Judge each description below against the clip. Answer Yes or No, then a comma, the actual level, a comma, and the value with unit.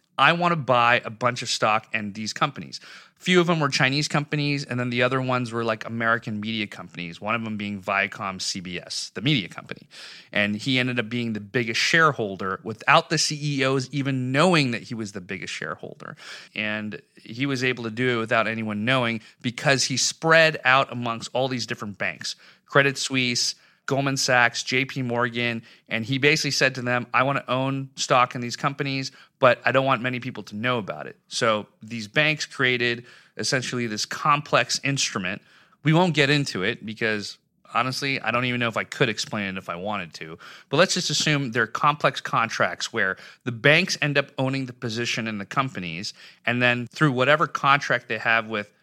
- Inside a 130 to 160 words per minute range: No, average, 195 wpm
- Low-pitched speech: Yes, low, 125 Hz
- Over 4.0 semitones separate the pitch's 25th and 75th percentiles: No, average, 3.5 semitones